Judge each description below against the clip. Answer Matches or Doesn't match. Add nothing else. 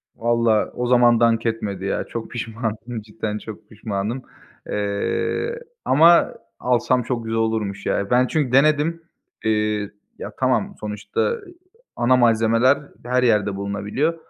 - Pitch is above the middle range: Doesn't match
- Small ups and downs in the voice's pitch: Doesn't match